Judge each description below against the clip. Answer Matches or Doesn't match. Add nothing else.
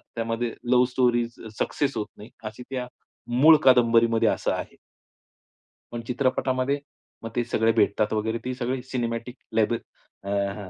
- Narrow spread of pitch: Matches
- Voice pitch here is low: Matches